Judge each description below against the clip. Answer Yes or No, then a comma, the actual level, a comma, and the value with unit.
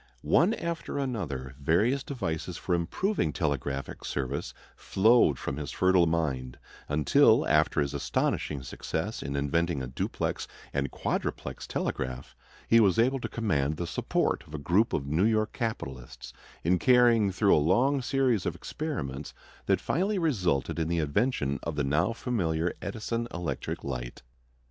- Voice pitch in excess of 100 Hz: No, very low, 85 Hz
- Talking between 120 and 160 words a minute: Yes, average, 150 wpm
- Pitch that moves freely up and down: Yes, wide, 8.5 semitones